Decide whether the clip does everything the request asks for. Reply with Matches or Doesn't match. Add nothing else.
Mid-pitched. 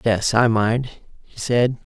Doesn't match